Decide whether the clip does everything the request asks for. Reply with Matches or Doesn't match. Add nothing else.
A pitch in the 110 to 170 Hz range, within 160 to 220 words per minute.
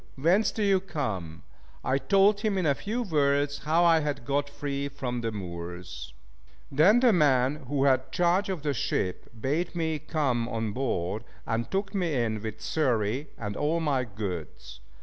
Matches